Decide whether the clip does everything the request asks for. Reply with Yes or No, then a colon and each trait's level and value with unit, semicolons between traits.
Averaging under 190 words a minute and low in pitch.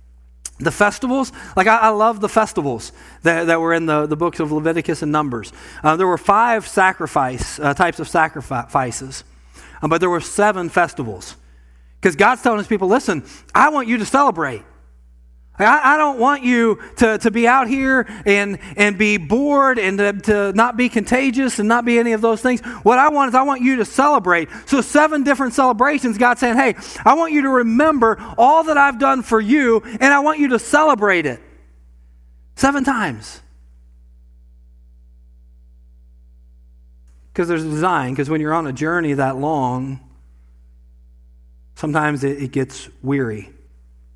No: average, 170 wpm; medium, 175 Hz